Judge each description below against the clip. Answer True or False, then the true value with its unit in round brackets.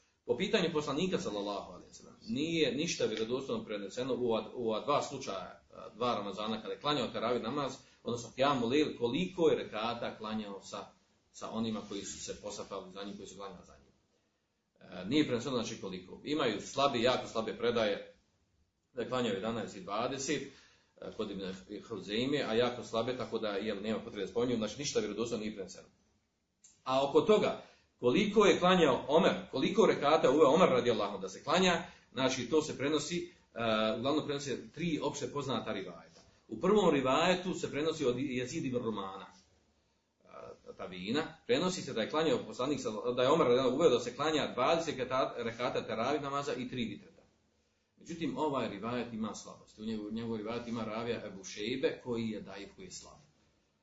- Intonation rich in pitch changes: True (5.8 semitones)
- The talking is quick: True (165 wpm)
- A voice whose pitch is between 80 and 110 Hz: False (125 Hz)